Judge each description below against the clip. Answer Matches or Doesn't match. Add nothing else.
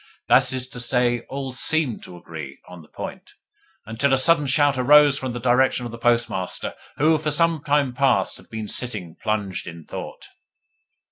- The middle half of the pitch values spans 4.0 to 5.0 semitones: Matches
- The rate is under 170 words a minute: Doesn't match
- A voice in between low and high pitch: Doesn't match